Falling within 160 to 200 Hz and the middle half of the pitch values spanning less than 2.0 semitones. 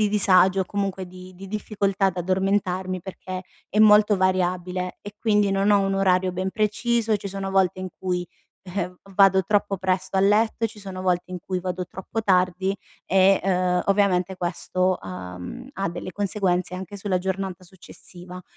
Yes: high, 190 Hz; narrow, 1.6 semitones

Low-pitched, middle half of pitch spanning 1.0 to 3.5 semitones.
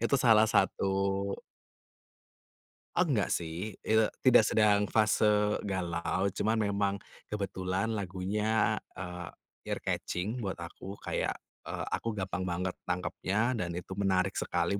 Yes: low, 100 Hz; average, 2.7 semitones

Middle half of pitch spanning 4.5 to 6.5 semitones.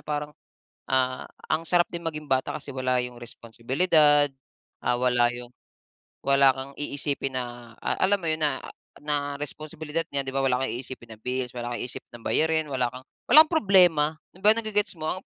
No: average, 3.8 semitones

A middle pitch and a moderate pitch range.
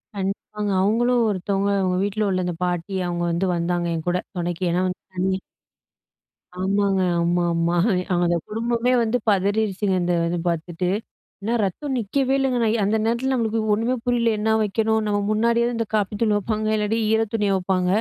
No: high, 205 Hz; average, 3.7 semitones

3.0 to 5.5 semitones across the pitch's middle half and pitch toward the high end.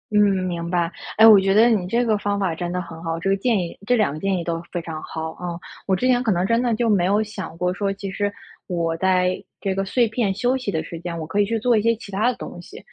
Yes: average, 3.9 semitones; high, 195 Hz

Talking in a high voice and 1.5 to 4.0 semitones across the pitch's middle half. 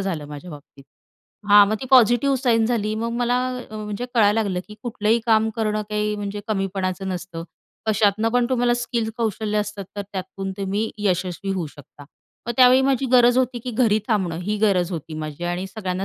Yes: high, 210 Hz; average, 3.5 semitones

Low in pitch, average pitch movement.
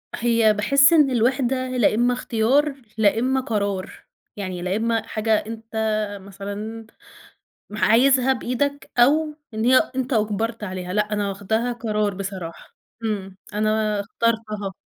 No: high, 220 Hz; average, 3.3 semitones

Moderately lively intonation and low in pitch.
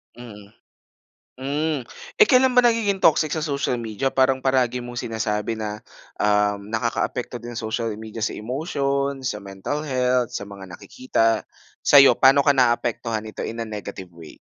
Yes: average, 4.4 semitones; low, 120 Hz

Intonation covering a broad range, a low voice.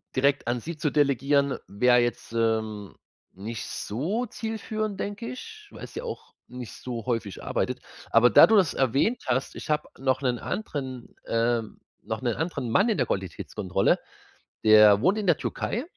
Yes: wide, 7.8 semitones; low, 130 Hz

